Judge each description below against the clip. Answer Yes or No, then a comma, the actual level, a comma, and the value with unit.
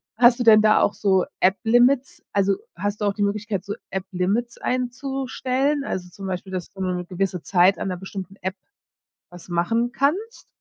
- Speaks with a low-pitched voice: No, high, 200 Hz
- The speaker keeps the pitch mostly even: No, average, 4.5 semitones